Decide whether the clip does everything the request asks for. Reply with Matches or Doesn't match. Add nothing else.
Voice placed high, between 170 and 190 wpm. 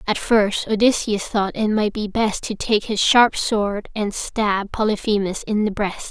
Matches